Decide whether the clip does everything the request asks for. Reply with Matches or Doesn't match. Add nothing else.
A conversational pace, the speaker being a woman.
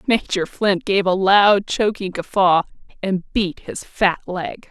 Matches